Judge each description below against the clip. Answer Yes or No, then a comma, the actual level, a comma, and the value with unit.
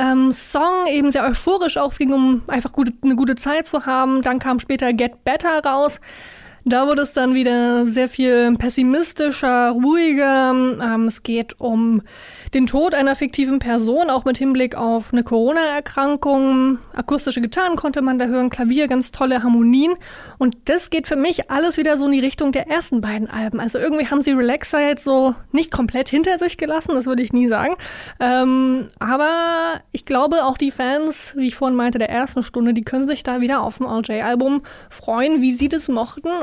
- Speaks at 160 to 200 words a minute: Yes, fast, 190 wpm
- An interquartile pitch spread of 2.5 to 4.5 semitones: Yes, average, 2.8 semitones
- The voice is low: No, very high, 265 Hz